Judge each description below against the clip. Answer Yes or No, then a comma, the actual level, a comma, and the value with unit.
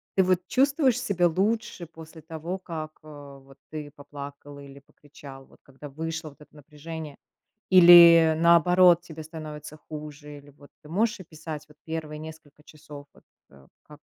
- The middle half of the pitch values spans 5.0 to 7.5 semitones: No, average, 2.7 semitones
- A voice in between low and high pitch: Yes, medium, 155 Hz